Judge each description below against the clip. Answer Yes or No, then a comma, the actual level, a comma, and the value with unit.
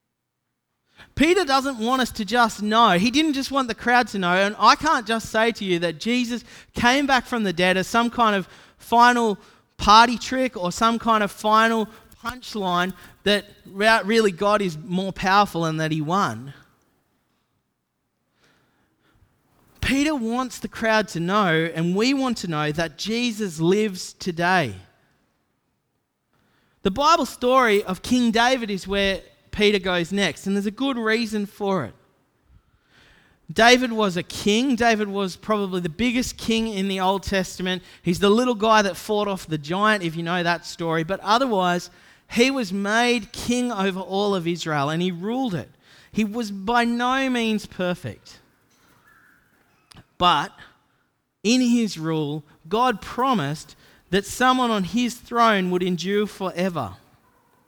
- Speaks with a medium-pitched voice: No, high, 210 Hz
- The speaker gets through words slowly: No, average, 155 wpm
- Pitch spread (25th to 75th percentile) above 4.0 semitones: Yes, average, 4.4 semitones